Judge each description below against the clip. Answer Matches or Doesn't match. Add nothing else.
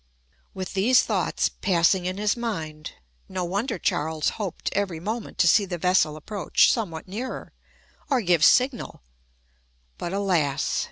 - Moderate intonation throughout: Matches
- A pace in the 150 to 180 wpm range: Doesn't match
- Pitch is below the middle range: Doesn't match